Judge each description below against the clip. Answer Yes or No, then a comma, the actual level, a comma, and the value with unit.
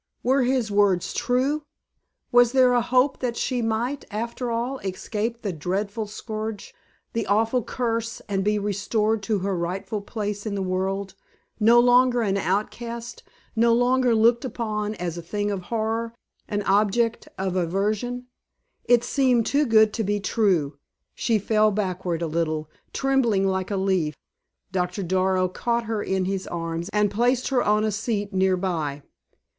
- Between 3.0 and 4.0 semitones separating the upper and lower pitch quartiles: Yes, average, 3.6 semitones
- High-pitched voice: Yes, high, 210 Hz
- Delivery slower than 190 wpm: Yes, average, 160 wpm